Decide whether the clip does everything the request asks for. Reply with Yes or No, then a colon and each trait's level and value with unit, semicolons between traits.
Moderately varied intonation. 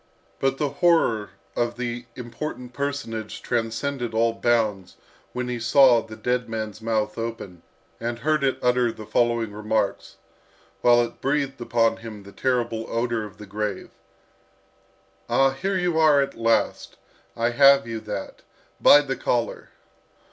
Yes: average, 3.1 semitones